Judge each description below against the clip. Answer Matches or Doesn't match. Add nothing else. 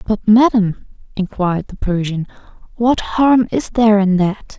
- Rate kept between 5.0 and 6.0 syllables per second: Doesn't match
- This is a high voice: Matches